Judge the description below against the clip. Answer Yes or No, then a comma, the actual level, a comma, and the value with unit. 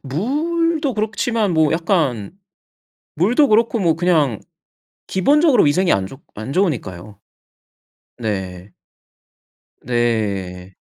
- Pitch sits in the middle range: Yes, medium, 160 Hz